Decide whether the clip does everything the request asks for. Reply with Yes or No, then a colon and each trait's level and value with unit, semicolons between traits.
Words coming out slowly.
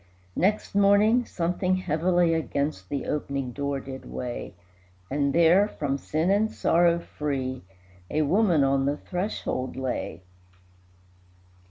Yes: slow, 120 wpm